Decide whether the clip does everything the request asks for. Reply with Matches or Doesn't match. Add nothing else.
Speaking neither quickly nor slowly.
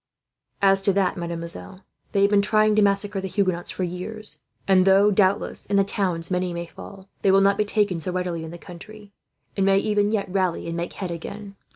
Doesn't match